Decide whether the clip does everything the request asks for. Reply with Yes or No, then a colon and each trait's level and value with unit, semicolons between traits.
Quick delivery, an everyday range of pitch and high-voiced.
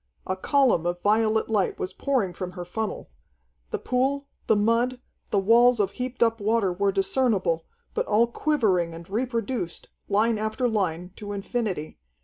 No: average, 155 wpm; average, 4.1 semitones; high, 215 Hz